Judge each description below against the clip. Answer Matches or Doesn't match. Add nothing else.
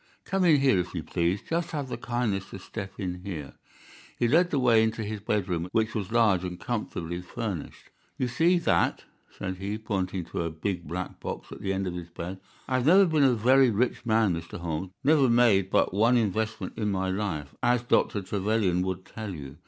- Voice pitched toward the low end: Matches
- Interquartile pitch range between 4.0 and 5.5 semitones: Matches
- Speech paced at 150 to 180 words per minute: Doesn't match